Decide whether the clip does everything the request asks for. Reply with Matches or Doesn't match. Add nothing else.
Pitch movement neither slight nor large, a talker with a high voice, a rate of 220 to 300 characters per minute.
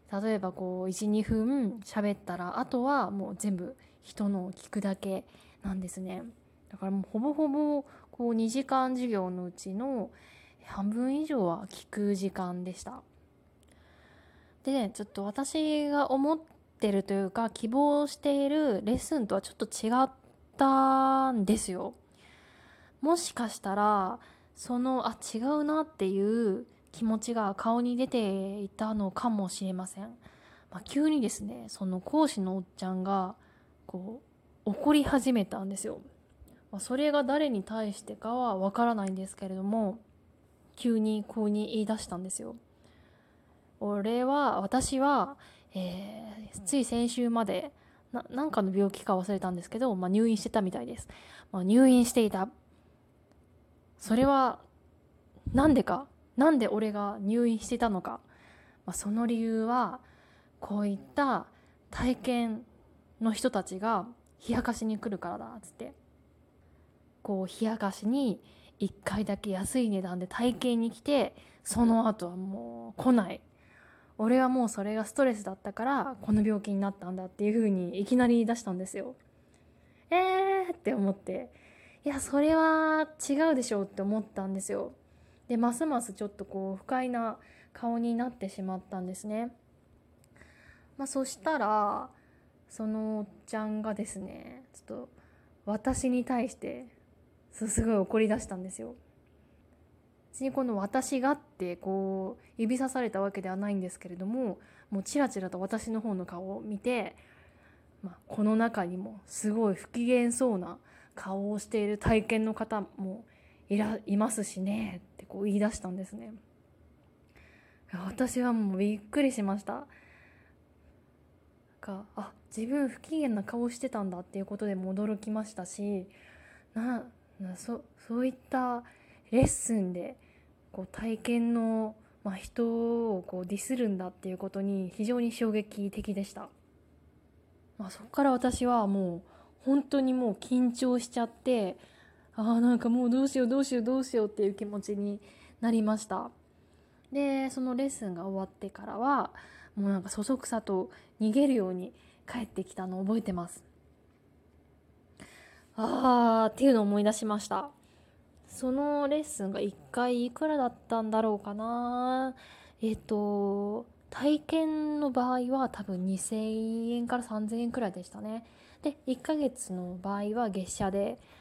Matches